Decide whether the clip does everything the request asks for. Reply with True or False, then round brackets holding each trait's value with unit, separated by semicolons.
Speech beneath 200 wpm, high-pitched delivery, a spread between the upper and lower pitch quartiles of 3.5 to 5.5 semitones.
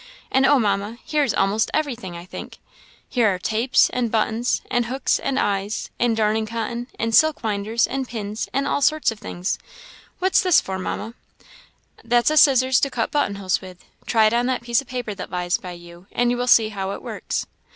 False (205 wpm; 230 Hz; 3.8 semitones)